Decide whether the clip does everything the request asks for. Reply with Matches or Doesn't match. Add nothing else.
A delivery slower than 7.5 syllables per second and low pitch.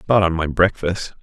Matches